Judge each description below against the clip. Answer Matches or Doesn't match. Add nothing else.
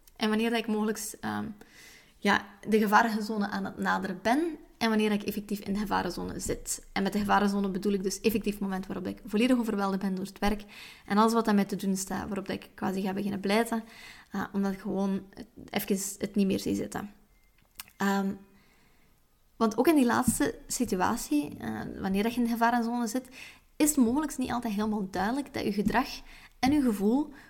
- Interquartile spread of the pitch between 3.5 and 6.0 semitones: Doesn't match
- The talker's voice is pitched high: Matches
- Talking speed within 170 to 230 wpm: Matches